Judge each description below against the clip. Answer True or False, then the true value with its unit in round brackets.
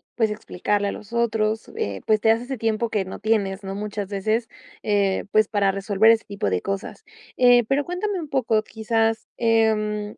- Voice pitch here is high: True (215 Hz)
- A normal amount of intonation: False (2.0 semitones)